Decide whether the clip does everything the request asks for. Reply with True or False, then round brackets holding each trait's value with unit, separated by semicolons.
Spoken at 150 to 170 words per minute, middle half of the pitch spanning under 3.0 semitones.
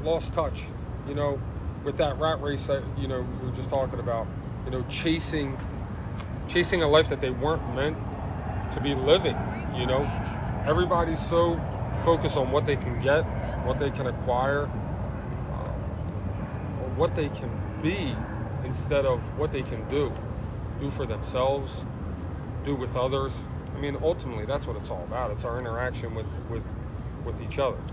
False (165 wpm; 3.8 semitones)